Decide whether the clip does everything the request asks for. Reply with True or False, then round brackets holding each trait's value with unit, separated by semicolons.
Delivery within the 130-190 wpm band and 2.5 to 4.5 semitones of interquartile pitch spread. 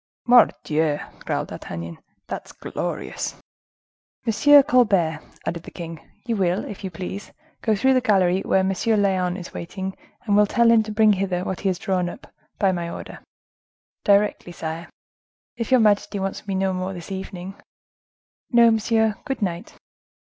True (155 wpm; 3.5 semitones)